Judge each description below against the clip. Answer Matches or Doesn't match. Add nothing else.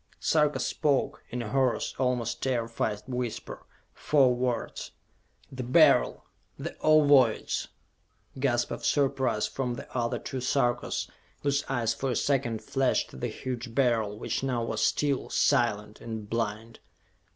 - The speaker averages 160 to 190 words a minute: Doesn't match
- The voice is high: Doesn't match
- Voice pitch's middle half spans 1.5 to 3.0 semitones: Matches